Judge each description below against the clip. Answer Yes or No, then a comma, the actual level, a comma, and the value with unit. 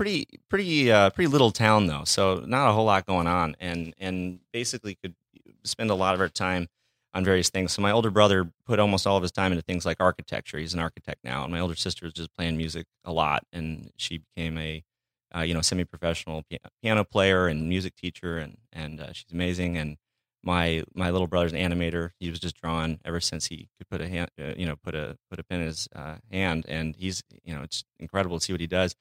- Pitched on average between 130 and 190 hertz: No, very low, 90 Hz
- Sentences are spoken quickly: Yes, fast, 240 wpm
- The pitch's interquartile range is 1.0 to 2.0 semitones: No, average, 2.7 semitones